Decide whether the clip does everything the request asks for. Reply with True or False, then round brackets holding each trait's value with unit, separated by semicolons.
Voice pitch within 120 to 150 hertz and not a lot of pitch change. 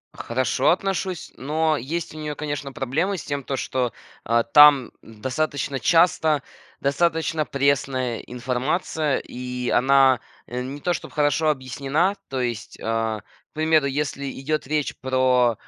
False (140 Hz; 3.3 semitones)